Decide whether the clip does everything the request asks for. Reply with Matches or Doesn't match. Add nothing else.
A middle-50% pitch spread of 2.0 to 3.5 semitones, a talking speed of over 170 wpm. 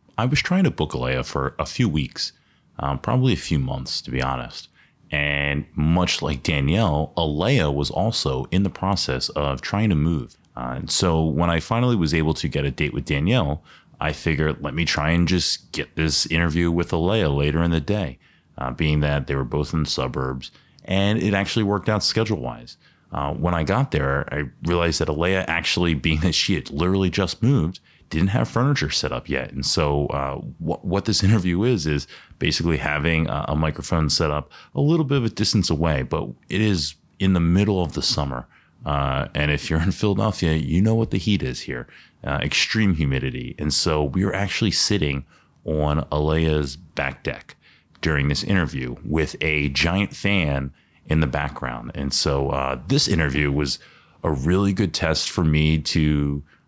Doesn't match